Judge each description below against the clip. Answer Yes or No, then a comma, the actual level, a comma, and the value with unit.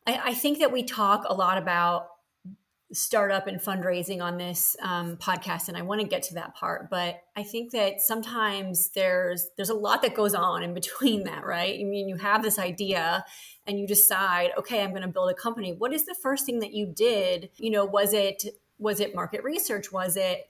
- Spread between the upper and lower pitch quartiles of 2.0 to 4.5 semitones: Yes, average, 3.1 semitones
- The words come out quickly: Yes, fast, 215 wpm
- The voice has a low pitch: No, high, 200 Hz